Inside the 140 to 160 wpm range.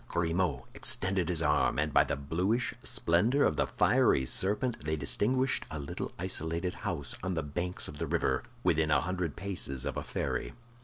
No: average, 175 wpm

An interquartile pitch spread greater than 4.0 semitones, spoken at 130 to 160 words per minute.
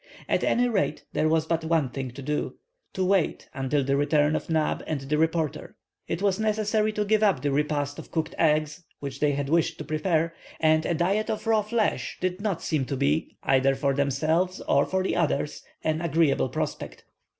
No: average, 4.4 semitones; average, 195 wpm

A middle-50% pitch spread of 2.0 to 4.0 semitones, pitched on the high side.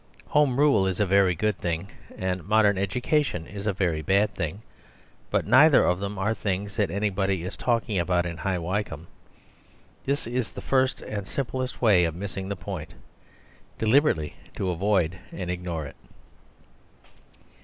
No: average, 3.4 semitones; low, 100 Hz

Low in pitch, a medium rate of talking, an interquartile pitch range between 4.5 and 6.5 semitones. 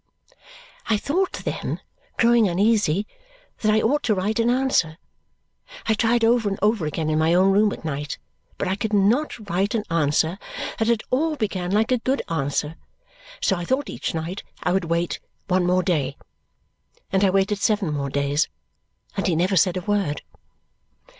No: high, 195 Hz; average, 175 wpm; average, 4.8 semitones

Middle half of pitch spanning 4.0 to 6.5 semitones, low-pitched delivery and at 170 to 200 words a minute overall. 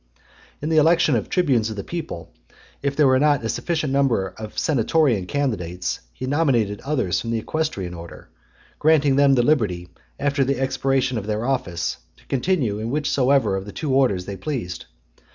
Yes: wide, 5.6 semitones; low, 130 Hz; average, 180 wpm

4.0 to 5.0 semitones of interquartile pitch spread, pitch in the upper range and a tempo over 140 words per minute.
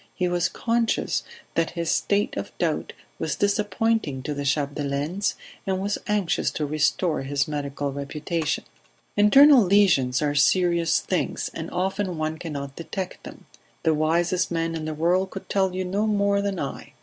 No: average, 4.5 semitones; medium, 170 Hz; average, 160 wpm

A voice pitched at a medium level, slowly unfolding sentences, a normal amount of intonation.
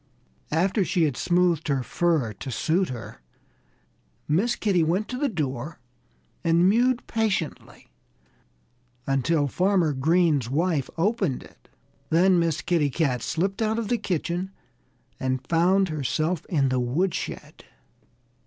Yes: medium, 170 Hz; slow, 125 wpm; average, 4.9 semitones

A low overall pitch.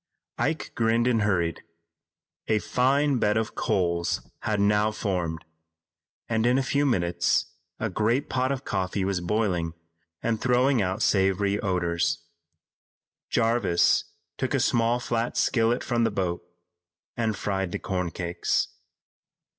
Yes: low, 105 Hz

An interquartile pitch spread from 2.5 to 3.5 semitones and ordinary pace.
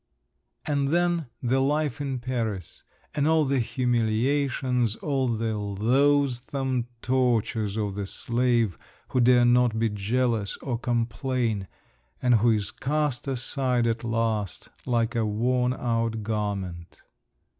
No: average, 2.9 semitones; slow, 125 wpm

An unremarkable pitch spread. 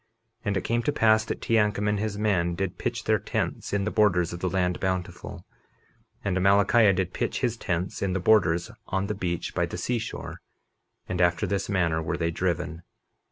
Yes: average, 3.1 semitones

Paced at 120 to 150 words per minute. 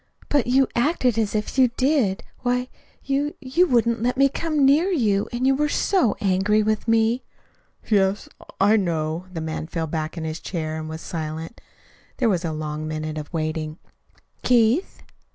No: average, 170 wpm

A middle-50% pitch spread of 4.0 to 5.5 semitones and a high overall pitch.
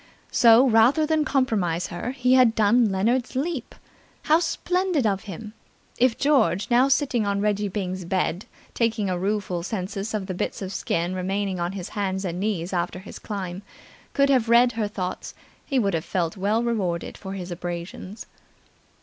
Yes: average, 4.6 semitones; high, 205 Hz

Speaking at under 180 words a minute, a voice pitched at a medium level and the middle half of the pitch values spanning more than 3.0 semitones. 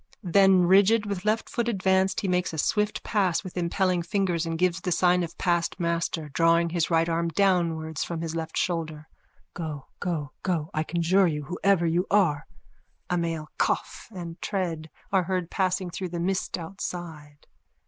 No: average, 170 wpm; medium, 175 Hz; narrow, 2.4 semitones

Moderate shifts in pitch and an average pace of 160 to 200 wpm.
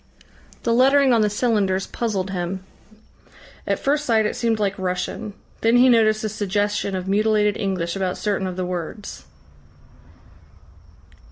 No: average, 3.0 semitones; average, 145 wpm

